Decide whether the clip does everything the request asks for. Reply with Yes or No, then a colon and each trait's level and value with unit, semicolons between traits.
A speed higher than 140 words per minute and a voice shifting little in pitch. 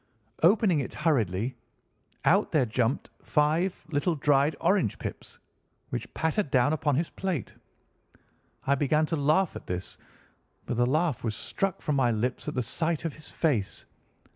No: average, 155 wpm; average, 4.5 semitones